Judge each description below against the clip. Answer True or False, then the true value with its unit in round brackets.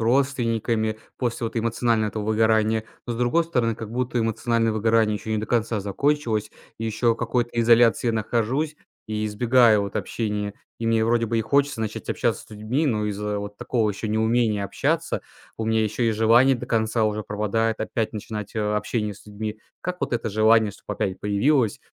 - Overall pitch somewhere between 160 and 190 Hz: False (110 Hz)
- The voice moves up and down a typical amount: False (1.7 semitones)